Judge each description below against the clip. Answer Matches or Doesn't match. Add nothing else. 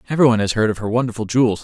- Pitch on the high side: Doesn't match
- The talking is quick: Matches